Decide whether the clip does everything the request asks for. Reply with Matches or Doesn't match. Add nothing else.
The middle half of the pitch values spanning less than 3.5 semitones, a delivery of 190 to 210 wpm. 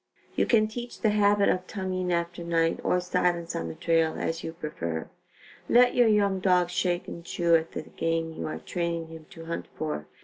Matches